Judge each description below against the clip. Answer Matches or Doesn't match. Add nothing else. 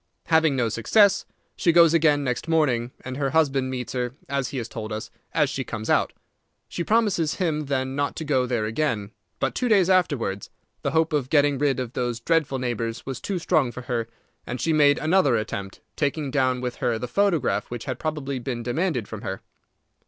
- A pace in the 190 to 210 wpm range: Matches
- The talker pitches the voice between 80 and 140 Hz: Matches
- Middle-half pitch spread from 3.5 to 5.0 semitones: Matches